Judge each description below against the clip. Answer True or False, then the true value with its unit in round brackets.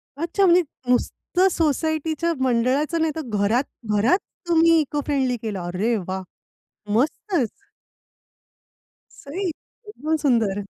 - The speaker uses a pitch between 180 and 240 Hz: False (285 Hz)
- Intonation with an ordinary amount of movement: False (6.0 semitones)